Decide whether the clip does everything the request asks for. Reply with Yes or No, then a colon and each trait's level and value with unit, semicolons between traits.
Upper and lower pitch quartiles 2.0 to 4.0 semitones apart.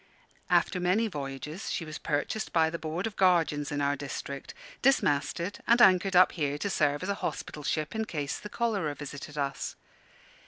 No: average, 4.9 semitones